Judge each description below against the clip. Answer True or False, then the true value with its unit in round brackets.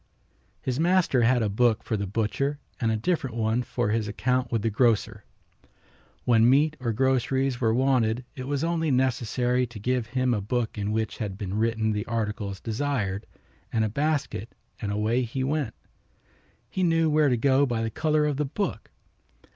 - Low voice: True (120 Hz)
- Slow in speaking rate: False (180 wpm)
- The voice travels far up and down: False (3.5 semitones)